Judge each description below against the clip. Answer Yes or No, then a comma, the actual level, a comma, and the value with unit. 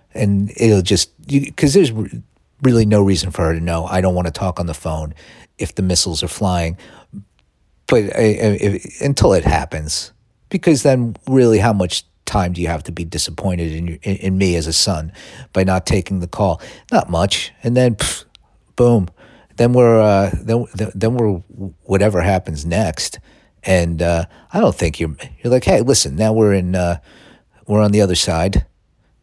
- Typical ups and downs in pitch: Yes, average, 4.3 semitones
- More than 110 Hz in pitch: No, very low, 95 Hz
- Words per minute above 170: Yes, average, 185 wpm